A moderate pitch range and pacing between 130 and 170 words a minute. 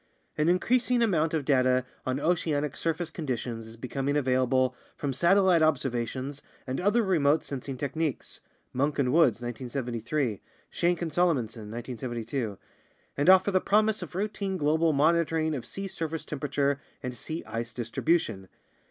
Yes: average, 4.9 semitones; average, 145 wpm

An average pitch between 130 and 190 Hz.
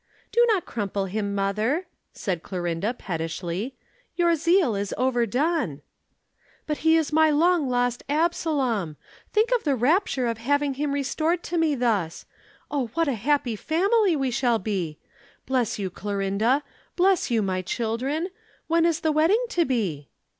No: very high, 260 Hz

